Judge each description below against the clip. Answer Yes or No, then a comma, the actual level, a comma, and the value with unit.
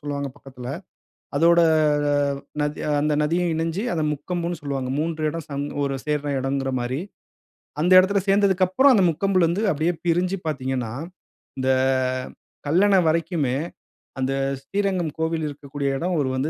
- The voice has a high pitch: No, medium, 160 Hz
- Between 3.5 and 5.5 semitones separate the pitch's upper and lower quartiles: Yes, average, 4.1 semitones